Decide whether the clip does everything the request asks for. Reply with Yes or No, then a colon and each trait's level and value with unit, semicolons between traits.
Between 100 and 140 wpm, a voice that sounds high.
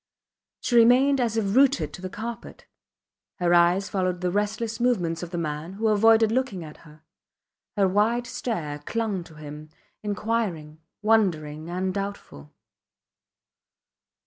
Yes: slow, 135 wpm; high, 195 Hz